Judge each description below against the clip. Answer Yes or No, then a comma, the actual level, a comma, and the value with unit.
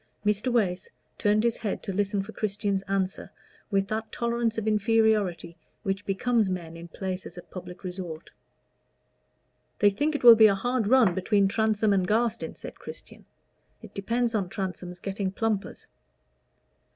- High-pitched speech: Yes, high, 205 Hz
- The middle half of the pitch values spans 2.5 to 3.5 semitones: Yes, average, 2.9 semitones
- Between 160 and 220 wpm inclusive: No, average, 150 wpm